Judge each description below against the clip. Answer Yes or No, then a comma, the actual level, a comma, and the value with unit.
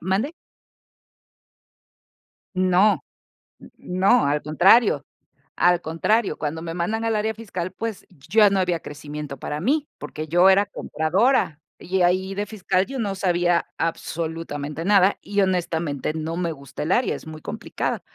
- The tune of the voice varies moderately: Yes, average, 4.0 semitones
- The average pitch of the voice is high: No, medium, 180 Hz